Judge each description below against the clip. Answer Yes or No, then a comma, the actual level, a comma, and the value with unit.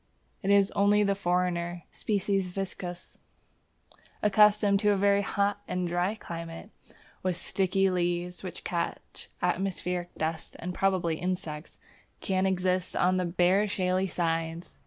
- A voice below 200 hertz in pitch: Yes, medium, 185 Hz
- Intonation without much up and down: Yes, narrow, 2.1 semitones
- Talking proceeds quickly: No, slow, 135 wpm